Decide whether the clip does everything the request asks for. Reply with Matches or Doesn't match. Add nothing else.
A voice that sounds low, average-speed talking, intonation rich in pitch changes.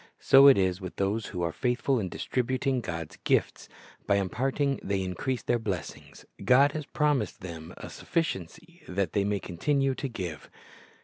Matches